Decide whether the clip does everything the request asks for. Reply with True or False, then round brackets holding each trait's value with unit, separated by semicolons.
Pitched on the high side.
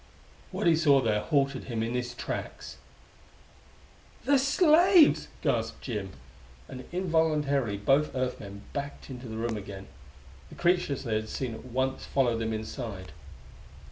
False (130 Hz)